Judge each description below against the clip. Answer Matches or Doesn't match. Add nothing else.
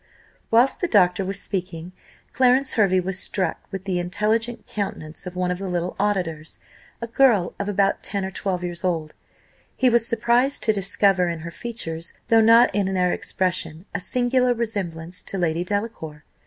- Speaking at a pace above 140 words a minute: Matches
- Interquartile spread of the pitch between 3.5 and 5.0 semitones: Matches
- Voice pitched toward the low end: Doesn't match